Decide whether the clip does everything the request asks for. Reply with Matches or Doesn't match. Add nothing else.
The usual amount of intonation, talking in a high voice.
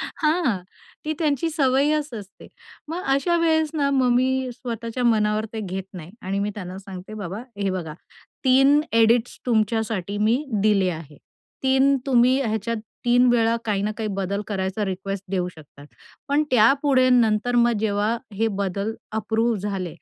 Matches